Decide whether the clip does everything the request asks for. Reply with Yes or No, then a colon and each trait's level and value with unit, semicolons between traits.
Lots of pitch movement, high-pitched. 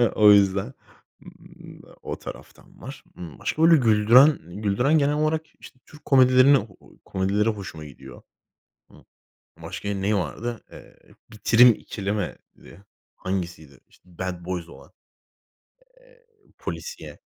No: wide, 6.0 semitones; low, 105 Hz